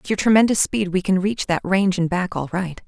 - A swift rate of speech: Yes, fast, 270 wpm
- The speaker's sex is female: Yes, female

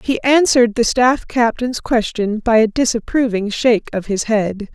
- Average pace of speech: Yes, average, 165 wpm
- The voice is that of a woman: Yes, female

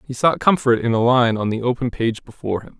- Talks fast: Yes, fast, 260 wpm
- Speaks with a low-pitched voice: Yes, low, 120 Hz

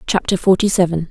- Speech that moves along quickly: No, average, 160 wpm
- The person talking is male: No, female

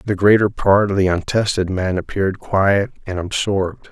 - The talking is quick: No, average, 170 wpm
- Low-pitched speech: Yes, very low, 95 Hz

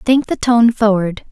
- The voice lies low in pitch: No, high, 225 Hz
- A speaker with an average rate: Yes, average, 185 wpm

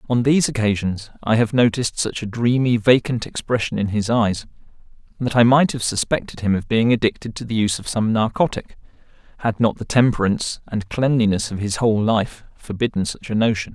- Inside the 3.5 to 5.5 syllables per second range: No, 5.7 syllables/s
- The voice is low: Yes, low, 115 Hz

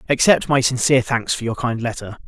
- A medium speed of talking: No, fast, 210 wpm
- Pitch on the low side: Yes, low, 125 Hz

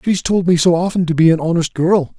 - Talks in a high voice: No, medium, 170 Hz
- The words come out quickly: Yes, fast, 275 wpm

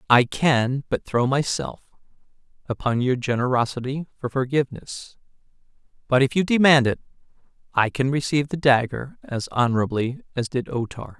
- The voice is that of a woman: No, male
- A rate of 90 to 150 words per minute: Yes, average, 140 wpm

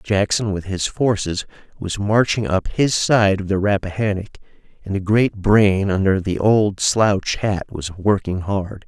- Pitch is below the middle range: Yes, low, 100 Hz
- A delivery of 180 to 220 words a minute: No, average, 160 wpm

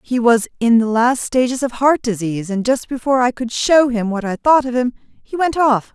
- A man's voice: No, female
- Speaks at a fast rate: Yes, fast, 240 wpm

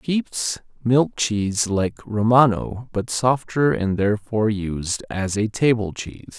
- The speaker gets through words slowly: Yes, slow, 130 wpm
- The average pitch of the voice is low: Yes, low, 110 Hz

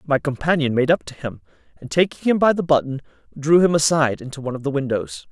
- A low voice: No, medium, 145 Hz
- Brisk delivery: Yes, fast, 225 wpm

